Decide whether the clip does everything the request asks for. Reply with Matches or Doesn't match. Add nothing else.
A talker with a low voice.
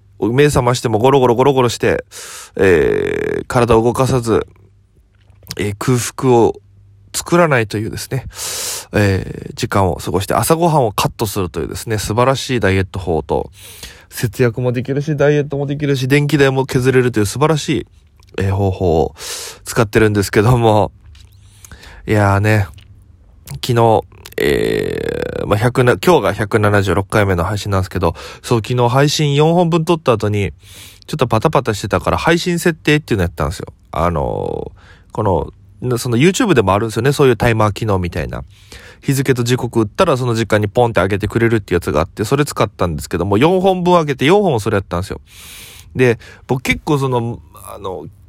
Matches